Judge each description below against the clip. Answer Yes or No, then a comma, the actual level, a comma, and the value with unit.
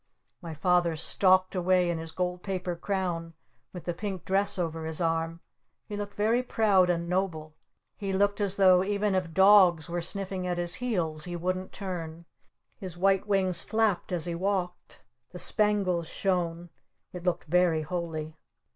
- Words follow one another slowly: No, average, 165 wpm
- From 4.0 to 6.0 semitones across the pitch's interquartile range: No, narrow, 2.4 semitones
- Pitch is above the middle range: No, medium, 180 Hz